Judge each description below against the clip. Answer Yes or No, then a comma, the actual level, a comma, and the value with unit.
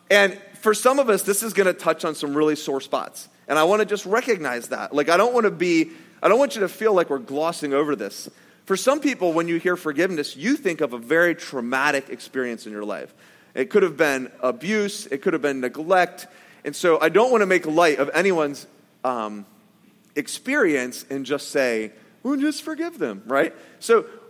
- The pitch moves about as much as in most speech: No, wide, 6.5 semitones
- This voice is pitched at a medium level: Yes, medium, 175 Hz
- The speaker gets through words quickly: Yes, fast, 210 wpm